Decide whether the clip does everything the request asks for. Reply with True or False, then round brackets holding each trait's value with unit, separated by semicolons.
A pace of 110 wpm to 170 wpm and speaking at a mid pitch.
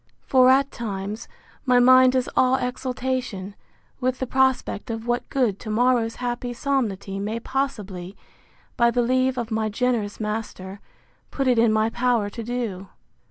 False (155 wpm; 240 Hz)